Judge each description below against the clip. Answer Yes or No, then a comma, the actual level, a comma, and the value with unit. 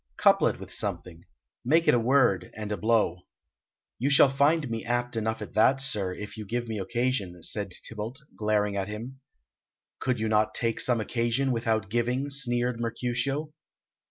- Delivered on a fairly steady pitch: No, average, 3.2 semitones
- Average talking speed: Yes, average, 170 wpm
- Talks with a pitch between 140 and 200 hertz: No, low, 115 Hz